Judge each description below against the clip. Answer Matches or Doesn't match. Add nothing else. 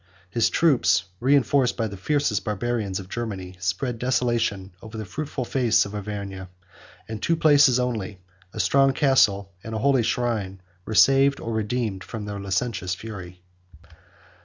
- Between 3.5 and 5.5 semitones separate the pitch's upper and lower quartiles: Matches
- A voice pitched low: Matches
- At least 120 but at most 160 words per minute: Matches